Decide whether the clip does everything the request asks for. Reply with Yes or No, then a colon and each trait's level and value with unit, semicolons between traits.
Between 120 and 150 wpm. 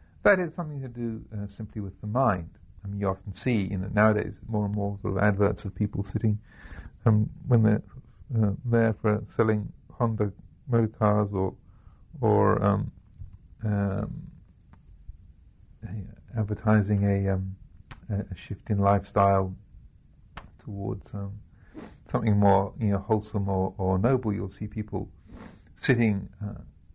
Yes: average, 145 wpm